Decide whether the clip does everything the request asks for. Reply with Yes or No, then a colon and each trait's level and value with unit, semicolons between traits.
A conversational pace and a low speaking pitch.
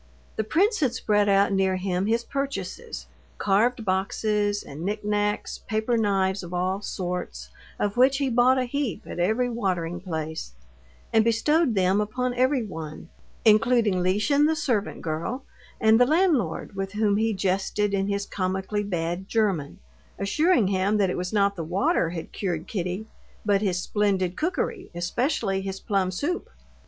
No: average, 155 wpm; high, 200 Hz